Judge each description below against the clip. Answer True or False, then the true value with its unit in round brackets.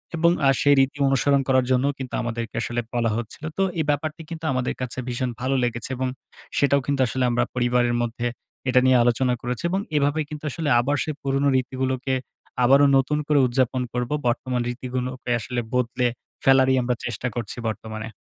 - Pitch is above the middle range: False (130 Hz)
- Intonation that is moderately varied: False (2.2 semitones)